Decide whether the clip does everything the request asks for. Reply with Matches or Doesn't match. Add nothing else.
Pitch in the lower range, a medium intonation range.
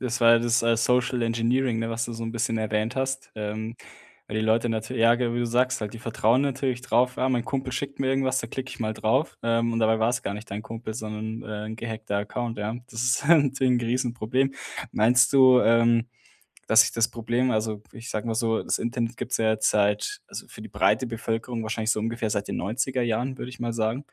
Doesn't match